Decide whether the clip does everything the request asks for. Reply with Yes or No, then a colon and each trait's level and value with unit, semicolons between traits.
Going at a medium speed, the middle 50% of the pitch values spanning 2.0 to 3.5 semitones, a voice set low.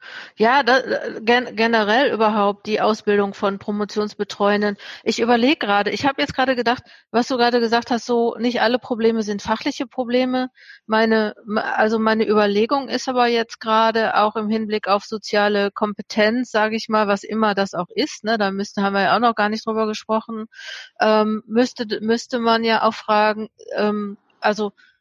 No: average, 175 wpm; narrow, 2.4 semitones; high, 220 Hz